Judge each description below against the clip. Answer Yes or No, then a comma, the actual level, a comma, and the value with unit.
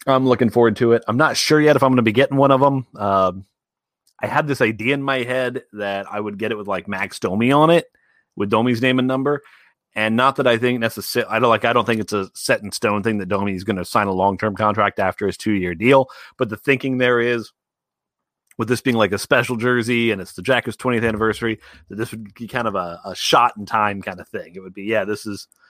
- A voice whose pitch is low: Yes, low, 115 Hz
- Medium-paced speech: No, fast, 265 wpm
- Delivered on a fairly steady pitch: No, average, 3.4 semitones